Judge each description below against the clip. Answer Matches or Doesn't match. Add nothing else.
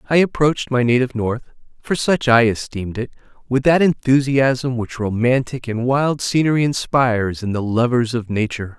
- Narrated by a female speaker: Doesn't match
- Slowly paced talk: Doesn't match